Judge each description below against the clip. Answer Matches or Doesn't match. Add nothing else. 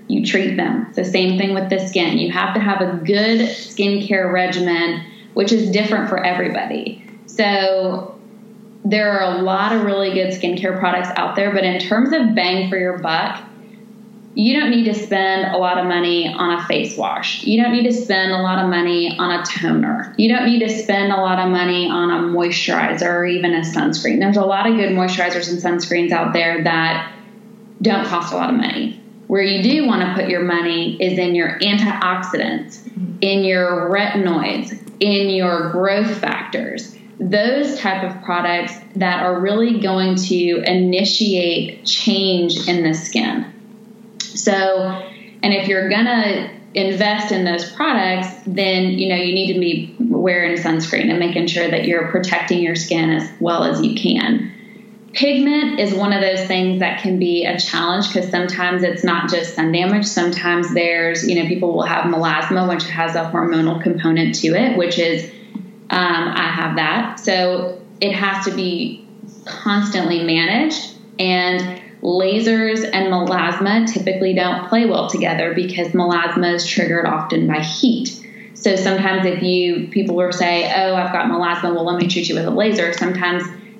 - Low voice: Doesn't match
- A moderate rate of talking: Matches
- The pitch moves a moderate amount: Matches